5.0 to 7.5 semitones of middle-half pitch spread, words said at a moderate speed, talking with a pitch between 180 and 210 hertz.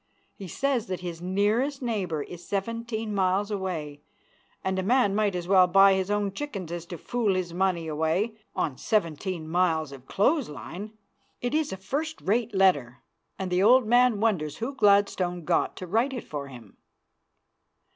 No: average, 4.3 semitones; average, 170 wpm; high, 190 Hz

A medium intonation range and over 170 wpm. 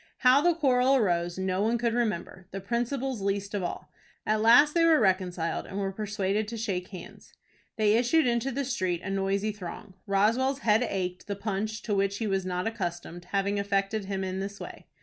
Yes: average, 3.7 semitones; average, 195 wpm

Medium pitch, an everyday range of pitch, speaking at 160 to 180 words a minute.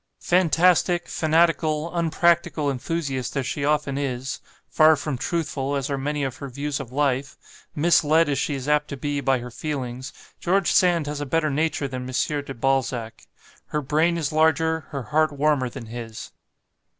Yes: medium, 145 Hz; average, 3.0 semitones; average, 170 wpm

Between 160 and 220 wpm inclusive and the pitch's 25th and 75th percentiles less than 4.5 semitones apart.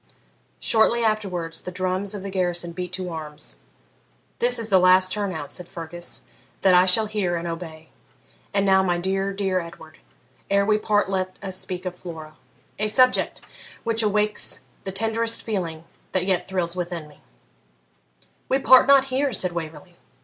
Yes: average, 165 wpm; average, 3.3 semitones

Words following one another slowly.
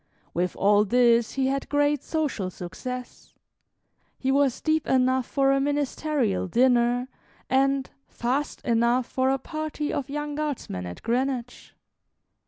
Yes: slow, 130 wpm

